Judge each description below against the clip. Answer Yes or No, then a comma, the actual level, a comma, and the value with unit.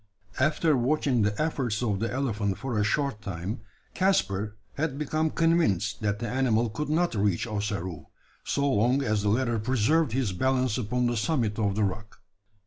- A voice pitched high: No, low, 115 Hz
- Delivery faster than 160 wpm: Yes, average, 170 wpm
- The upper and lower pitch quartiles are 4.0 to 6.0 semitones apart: Yes, average, 4.9 semitones